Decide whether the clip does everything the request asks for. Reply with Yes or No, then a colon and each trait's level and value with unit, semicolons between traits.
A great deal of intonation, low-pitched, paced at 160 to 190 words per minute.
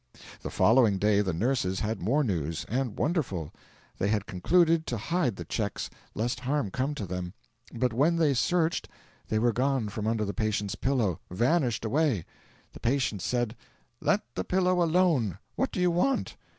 Yes: wide, 6.4 semitones; low, 120 Hz; average, 170 wpm